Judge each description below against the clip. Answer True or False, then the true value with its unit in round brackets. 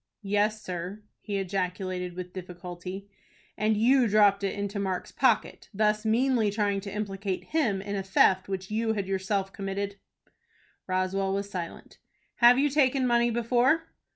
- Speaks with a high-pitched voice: True (200 Hz)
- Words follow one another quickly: False (150 wpm)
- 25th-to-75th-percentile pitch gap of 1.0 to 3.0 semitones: True (2.5 semitones)